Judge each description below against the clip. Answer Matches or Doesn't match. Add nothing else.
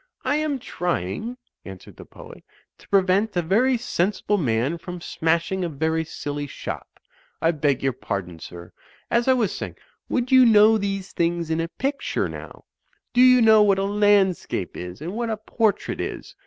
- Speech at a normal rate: Matches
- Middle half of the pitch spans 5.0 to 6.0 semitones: Matches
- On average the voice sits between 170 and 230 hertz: Matches